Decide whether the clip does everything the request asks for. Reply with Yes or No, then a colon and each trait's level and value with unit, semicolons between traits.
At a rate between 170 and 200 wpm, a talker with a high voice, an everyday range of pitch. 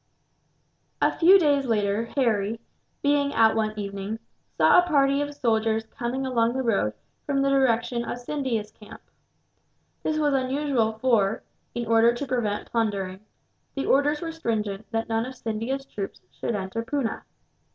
No: average, 150 wpm; high, 235 Hz; average, 3.9 semitones